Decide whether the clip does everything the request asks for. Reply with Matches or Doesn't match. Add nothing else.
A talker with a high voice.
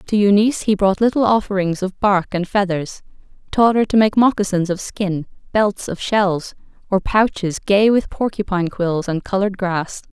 Matches